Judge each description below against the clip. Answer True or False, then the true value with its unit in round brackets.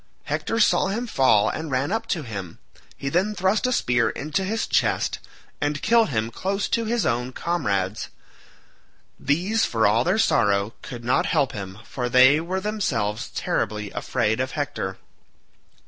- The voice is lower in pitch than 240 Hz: True (140 Hz)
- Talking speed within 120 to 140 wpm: False (160 wpm)